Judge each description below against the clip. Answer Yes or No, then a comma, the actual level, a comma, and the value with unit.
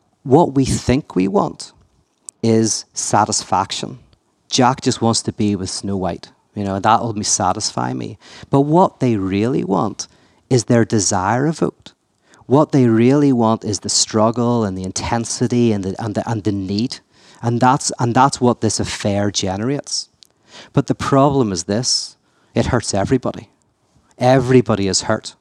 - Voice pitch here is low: Yes, low, 115 Hz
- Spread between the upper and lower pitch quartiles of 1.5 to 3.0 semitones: No, average, 3.8 semitones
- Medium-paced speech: Yes, average, 155 wpm